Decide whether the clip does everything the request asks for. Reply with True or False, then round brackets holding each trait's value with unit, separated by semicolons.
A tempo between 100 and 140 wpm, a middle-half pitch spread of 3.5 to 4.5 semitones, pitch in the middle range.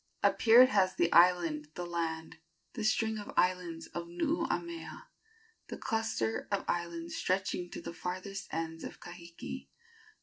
True (135 wpm; 3.8 semitones; 180 Hz)